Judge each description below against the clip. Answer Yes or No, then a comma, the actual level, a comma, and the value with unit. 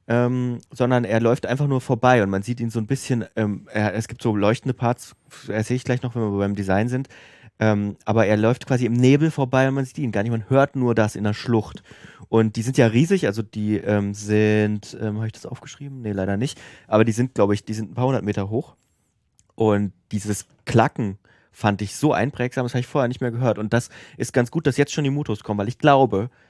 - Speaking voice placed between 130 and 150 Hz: No, low, 115 Hz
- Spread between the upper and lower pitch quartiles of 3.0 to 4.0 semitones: Yes, average, 3.3 semitones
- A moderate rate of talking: No, fast, 245 wpm